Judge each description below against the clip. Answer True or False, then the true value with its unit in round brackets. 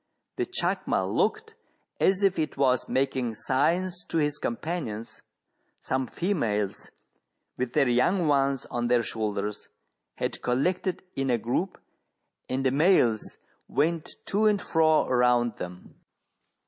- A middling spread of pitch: False (6.2 semitones)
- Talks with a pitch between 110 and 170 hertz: True (135 Hz)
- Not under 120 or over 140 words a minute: True (135 wpm)